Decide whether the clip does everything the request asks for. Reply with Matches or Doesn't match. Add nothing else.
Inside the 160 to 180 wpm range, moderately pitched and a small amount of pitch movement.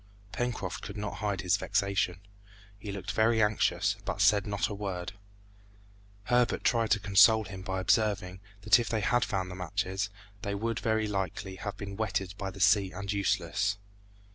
Doesn't match